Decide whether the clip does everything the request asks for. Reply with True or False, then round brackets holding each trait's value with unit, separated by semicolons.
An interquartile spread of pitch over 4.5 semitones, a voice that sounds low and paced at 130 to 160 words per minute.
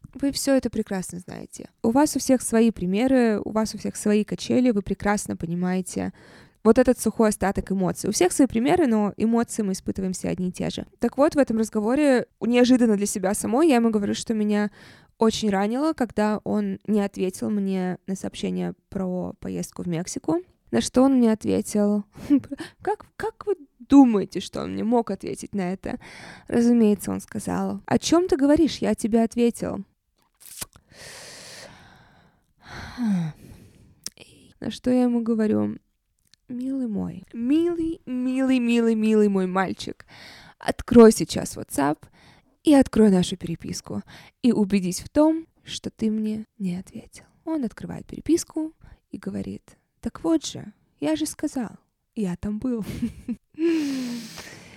False (4.9 semitones; 220 Hz; 145 wpm)